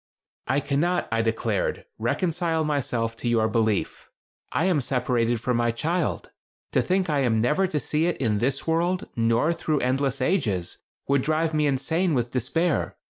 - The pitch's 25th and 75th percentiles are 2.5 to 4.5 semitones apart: No, wide, 5.6 semitones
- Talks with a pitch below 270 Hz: Yes, medium, 140 Hz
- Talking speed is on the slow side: No, average, 165 wpm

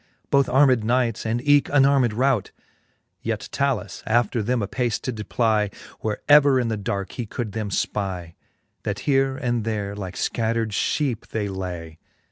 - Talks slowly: No, average, 155 wpm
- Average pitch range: Yes, average, 3.9 semitones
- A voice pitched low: Yes, low, 115 Hz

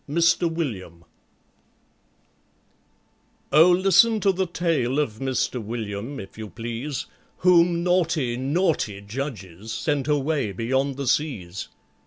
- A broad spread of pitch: Yes, wide, 6.9 semitones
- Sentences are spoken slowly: Yes, slow, 110 wpm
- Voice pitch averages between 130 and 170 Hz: Yes, low, 135 Hz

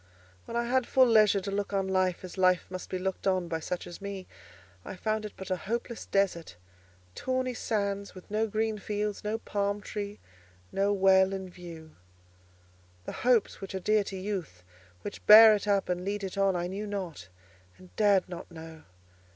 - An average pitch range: No, narrow, 2.3 semitones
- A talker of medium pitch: No, high, 195 Hz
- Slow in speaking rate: No, average, 190 wpm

